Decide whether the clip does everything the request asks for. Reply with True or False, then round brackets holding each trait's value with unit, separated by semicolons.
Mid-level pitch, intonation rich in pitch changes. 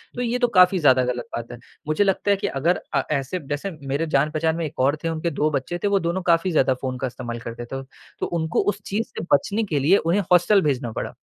True (160 Hz; 5.9 semitones)